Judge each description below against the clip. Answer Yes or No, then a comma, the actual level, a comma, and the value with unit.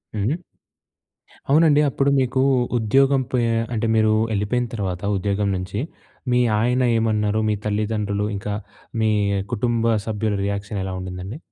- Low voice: Yes, low, 110 Hz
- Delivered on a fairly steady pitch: No, average, 3.1 semitones